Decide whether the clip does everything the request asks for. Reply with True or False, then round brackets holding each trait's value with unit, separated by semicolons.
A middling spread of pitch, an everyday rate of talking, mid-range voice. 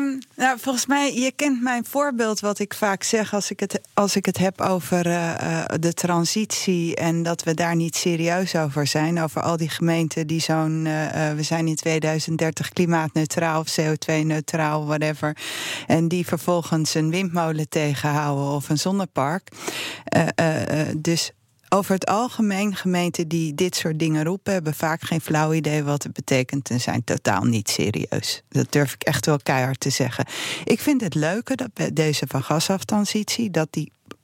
True (3.7 semitones; 175 wpm; 165 Hz)